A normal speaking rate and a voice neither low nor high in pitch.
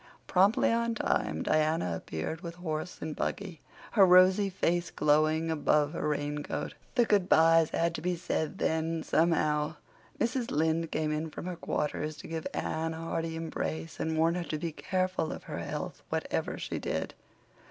Yes: average, 170 wpm; medium, 165 Hz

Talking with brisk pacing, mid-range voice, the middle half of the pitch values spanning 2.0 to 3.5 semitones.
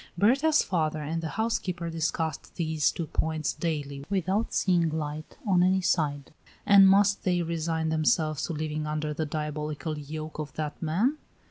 No: average, 155 wpm; medium, 160 Hz; average, 2.9 semitones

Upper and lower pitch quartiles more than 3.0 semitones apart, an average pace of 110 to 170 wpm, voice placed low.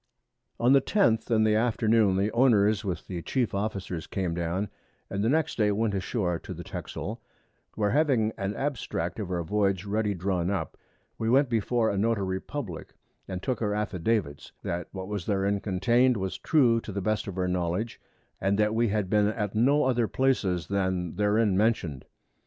No: average, 3.4 semitones; average, 185 wpm; low, 105 Hz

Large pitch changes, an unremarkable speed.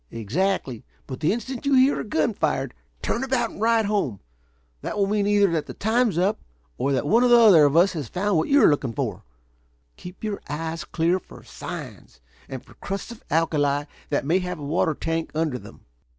No: wide, 6.3 semitones; fast, 210 wpm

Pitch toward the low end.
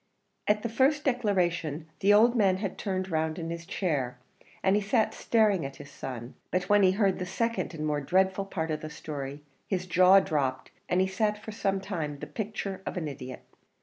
No: medium, 185 Hz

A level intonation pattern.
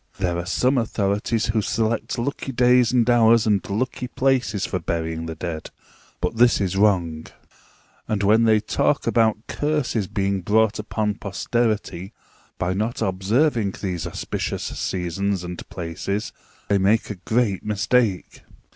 No: average, 3.6 semitones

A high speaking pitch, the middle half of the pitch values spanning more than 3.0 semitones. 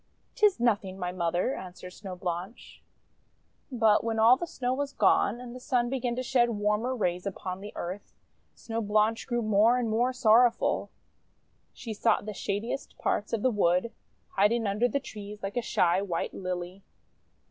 Yes: high, 215 Hz; average, 3.8 semitones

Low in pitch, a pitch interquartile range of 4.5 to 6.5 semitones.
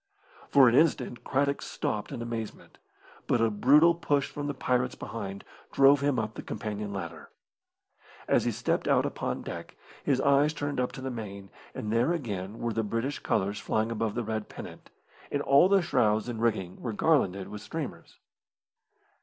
Yes: low, 120 Hz; average, 4.9 semitones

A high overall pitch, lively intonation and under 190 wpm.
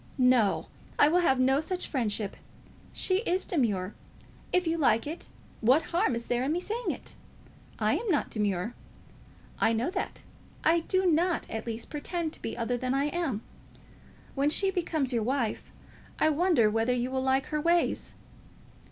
Yes: very high, 275 Hz; wide, 6.4 semitones; average, 170 wpm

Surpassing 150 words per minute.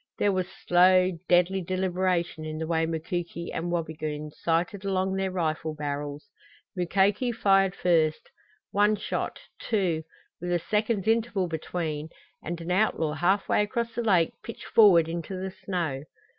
No: average, 145 wpm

